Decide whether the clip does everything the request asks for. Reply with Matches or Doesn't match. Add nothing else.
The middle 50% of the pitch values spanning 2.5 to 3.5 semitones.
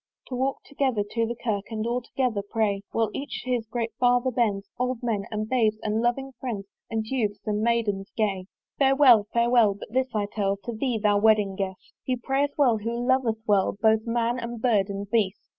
Matches